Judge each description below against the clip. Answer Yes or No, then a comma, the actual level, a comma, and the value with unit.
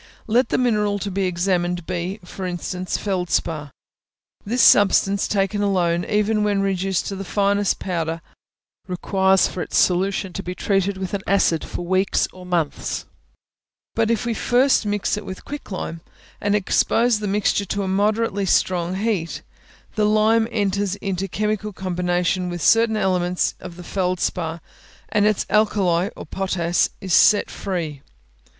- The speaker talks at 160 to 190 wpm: No, average, 150 wpm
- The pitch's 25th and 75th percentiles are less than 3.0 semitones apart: Yes, narrow, 2.6 semitones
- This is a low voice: No, high, 195 Hz